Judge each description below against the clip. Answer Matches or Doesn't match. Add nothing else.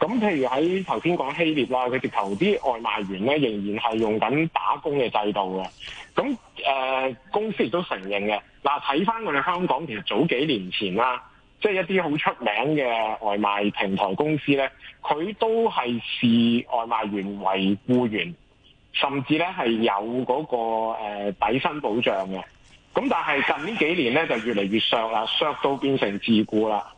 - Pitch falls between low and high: Doesn't match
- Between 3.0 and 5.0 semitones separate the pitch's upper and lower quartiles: Doesn't match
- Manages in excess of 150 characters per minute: Matches